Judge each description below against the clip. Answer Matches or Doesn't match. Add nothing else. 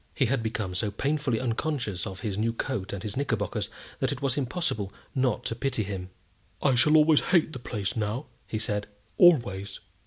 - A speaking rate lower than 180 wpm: Doesn't match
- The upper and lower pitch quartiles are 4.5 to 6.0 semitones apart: Matches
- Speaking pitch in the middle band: Doesn't match